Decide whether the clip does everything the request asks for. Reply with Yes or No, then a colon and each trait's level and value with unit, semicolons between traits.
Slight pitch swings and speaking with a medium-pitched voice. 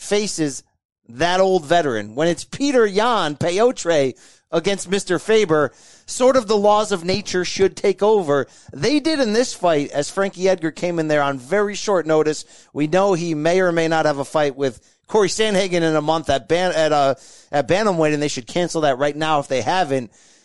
No: average, 5.1 semitones; medium, 170 Hz